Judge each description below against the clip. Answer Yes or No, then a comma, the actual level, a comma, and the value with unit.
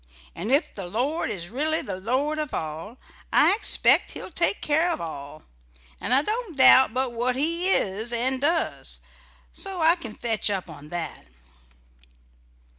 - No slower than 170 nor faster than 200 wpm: No, average, 160 wpm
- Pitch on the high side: Yes, very high, 255 Hz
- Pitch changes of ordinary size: No, wide, 7.9 semitones